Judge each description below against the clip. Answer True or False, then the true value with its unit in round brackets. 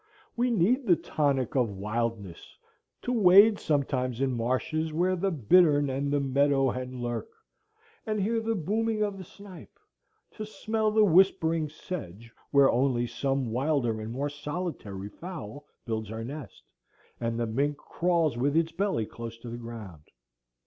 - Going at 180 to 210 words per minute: False (150 wpm)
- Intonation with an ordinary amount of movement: False (7.3 semitones)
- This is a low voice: False (145 Hz)